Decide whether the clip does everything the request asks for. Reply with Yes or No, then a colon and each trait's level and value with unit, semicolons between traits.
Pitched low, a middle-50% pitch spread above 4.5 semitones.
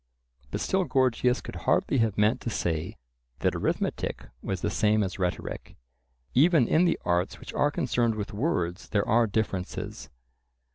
Yes: low, 110 Hz; average, 4.9 semitones